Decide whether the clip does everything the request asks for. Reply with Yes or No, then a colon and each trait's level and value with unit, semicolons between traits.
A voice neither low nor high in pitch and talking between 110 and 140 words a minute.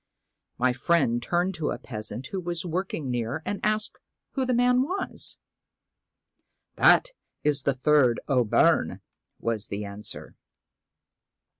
Yes: medium, 150 Hz; slow, 135 wpm